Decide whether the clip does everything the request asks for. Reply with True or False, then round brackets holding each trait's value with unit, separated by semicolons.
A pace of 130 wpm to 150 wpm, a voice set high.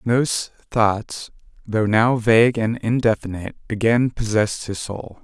False (140 wpm; 110 Hz)